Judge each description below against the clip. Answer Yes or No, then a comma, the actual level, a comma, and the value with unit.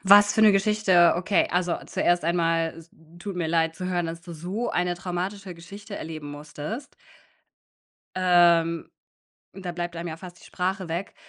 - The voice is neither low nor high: Yes, medium, 175 Hz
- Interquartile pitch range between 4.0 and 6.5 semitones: No, narrow, 2.4 semitones